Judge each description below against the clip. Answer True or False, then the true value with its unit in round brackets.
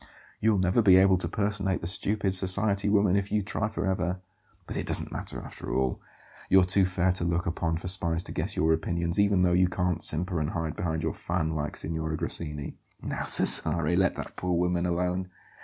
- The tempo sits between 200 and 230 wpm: True (205 wpm)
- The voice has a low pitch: True (90 Hz)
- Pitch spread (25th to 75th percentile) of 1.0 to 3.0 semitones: True (2.5 semitones)